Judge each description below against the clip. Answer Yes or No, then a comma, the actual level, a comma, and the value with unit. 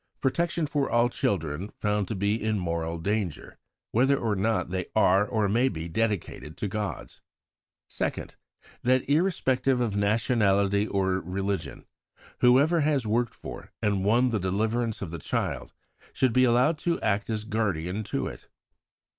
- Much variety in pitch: No, average, 4.0 semitones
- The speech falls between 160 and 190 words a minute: No, average, 150 wpm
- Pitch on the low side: Yes, low, 110 Hz